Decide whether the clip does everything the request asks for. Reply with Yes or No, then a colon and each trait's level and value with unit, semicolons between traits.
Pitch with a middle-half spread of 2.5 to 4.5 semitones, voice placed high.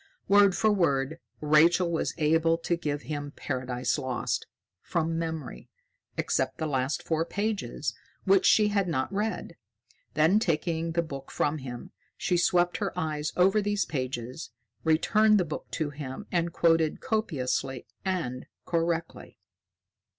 No: average, 3.9 semitones; medium, 160 Hz